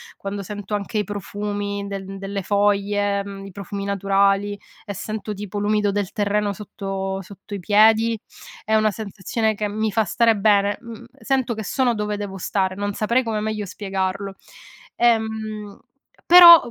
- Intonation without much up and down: Yes, narrow, 1.5 semitones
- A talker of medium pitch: No, high, 205 Hz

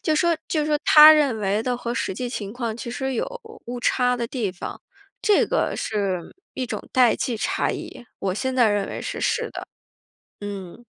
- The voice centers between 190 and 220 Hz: No, high, 240 Hz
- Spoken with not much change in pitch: No, average, 4.1 semitones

